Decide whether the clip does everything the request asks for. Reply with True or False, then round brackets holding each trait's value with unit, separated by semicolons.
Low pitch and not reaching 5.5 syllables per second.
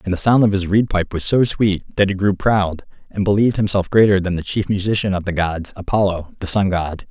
False (95 Hz; 5.6 syllables/s)